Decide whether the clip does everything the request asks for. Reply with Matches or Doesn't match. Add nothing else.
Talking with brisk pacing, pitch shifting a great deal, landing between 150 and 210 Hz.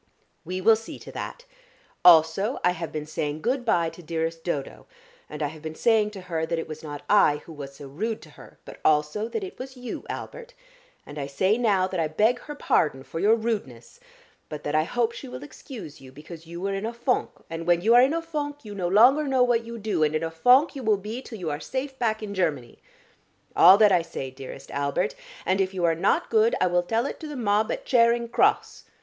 Matches